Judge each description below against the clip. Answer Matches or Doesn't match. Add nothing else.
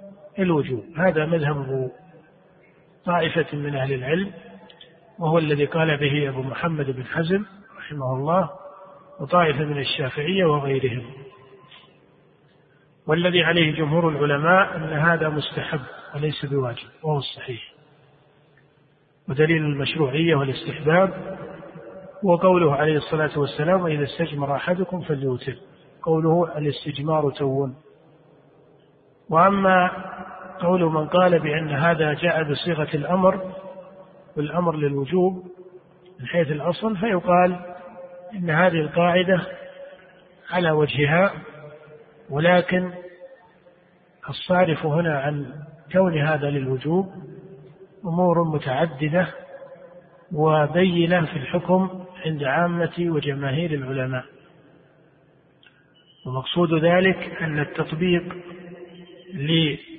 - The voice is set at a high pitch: Doesn't match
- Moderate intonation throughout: Matches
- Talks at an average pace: Matches